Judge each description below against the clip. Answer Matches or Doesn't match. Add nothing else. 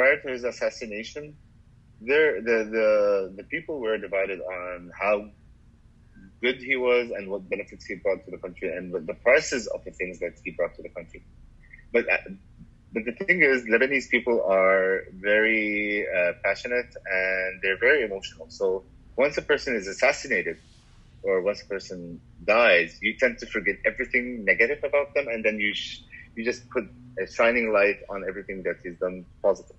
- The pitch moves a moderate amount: Doesn't match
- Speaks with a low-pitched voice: Matches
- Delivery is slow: Doesn't match